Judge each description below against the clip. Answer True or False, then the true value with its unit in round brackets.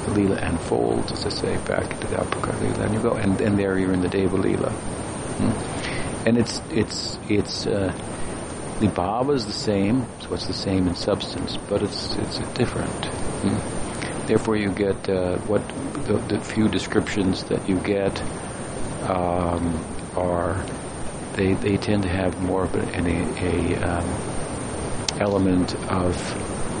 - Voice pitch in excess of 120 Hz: False (95 Hz)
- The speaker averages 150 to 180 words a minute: True (155 wpm)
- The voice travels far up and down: False (2.9 semitones)